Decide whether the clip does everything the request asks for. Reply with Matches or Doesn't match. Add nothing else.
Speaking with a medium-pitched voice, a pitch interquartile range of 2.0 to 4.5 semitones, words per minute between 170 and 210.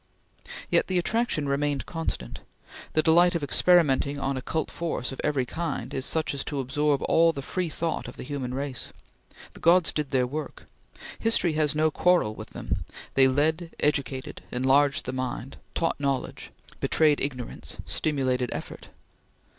Doesn't match